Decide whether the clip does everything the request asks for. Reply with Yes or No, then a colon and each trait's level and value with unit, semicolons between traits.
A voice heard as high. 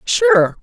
Yes: high, 200 Hz